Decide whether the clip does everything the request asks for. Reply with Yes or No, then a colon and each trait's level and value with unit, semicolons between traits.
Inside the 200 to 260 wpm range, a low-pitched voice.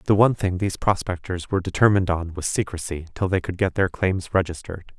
Yes: fast, 205 wpm; very low, 90 Hz